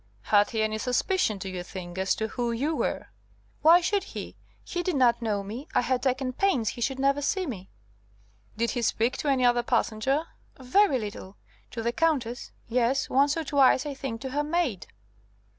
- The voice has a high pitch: Yes, very high, 250 Hz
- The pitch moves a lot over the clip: No, average, 4.3 semitones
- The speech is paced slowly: No, average, 195 wpm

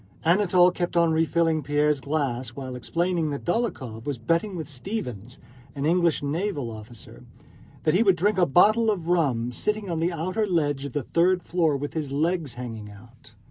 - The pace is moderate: Yes, average, 180 wpm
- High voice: No, medium, 160 Hz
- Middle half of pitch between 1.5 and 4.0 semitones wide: No, average, 4.9 semitones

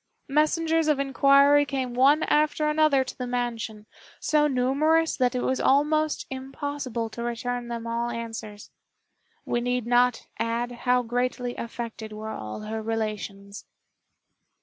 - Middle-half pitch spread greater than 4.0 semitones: No, average, 3.4 semitones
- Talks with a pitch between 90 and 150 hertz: No, high, 245 Hz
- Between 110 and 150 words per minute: Yes, slow, 135 wpm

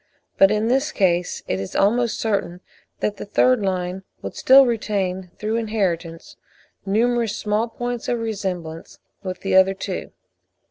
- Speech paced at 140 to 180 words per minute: Yes, average, 145 wpm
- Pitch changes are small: No, average, 3.7 semitones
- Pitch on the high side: Yes, high, 205 Hz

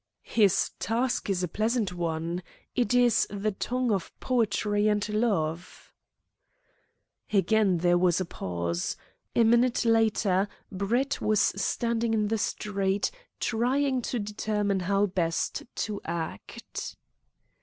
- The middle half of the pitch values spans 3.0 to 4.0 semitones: Yes, average, 3.6 semitones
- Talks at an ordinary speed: No, slow, 120 wpm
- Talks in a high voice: Yes, high, 205 Hz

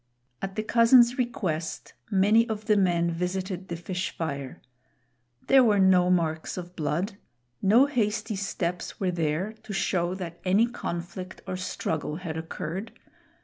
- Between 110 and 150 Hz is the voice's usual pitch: No, medium, 185 Hz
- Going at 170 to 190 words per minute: No, average, 145 wpm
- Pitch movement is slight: No, average, 3.7 semitones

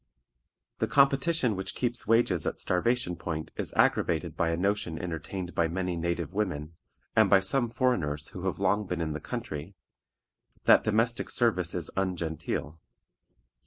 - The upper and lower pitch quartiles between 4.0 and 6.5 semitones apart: Yes, average, 5.1 semitones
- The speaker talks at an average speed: Yes, average, 150 wpm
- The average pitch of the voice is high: No, very low, 90 Hz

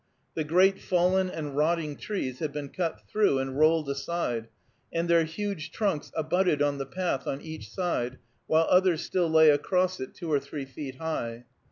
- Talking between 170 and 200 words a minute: Yes, average, 180 wpm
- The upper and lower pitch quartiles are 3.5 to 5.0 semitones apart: Yes, average, 4.2 semitones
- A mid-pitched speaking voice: Yes, medium, 160 Hz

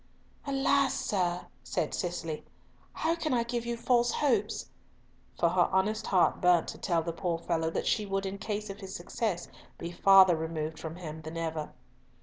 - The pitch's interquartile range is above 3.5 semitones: Yes, average, 4.7 semitones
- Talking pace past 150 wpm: Yes, average, 175 wpm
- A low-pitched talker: No, medium, 185 Hz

